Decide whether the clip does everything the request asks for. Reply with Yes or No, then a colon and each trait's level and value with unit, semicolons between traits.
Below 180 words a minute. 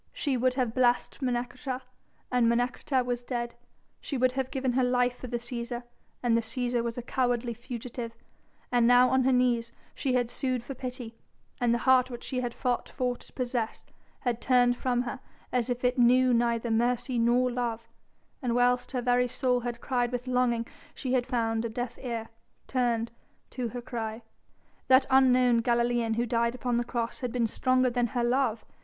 No: average, 185 wpm